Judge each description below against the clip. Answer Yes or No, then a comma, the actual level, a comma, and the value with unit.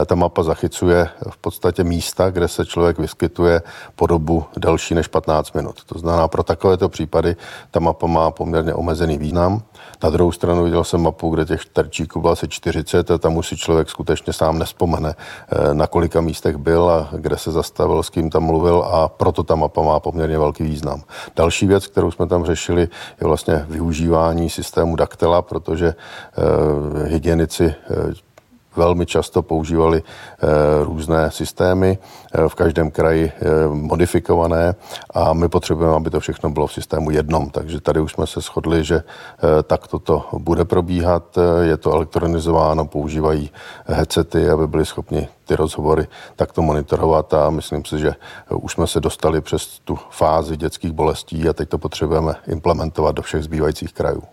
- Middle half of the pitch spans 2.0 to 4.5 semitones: No, narrow, 1.5 semitones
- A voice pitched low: Yes, very low, 80 Hz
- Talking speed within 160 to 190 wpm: Yes, average, 165 wpm